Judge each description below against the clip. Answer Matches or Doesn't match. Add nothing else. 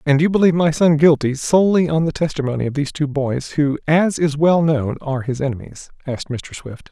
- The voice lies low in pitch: Doesn't match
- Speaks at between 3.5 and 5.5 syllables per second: Doesn't match